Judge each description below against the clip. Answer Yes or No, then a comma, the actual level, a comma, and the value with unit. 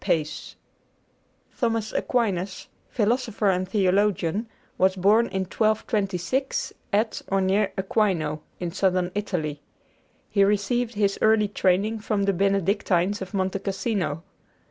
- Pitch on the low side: No, high, 200 Hz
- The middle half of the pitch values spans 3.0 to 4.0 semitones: No, narrow, 2.5 semitones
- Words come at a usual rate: No, slow, 115 wpm